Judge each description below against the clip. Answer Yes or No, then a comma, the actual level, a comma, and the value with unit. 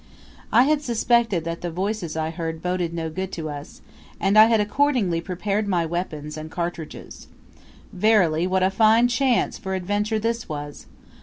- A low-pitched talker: No, medium, 185 Hz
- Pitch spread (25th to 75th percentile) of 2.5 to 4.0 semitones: No, average, 4.7 semitones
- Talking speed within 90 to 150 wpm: No, average, 165 wpm